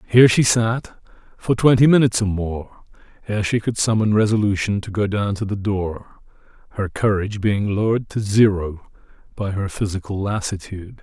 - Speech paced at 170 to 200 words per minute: No, average, 160 wpm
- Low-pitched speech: Yes, low, 105 Hz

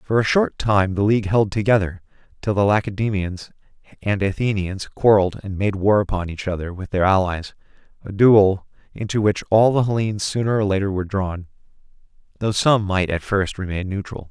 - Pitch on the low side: Yes, low, 100 Hz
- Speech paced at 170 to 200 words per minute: Yes, average, 175 wpm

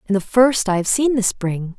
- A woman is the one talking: Yes, female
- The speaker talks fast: Yes, fast, 270 wpm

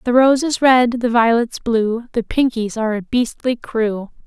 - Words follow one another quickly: No, average, 185 wpm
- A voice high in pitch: Yes, high, 235 Hz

